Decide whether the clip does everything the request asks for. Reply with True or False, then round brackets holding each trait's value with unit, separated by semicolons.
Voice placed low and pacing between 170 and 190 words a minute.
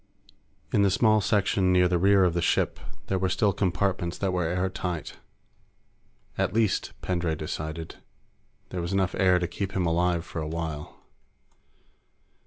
False (90 Hz; 155 wpm)